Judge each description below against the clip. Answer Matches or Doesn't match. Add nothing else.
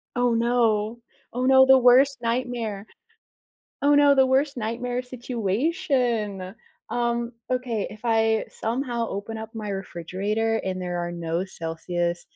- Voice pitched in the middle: Doesn't match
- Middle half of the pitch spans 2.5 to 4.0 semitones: Matches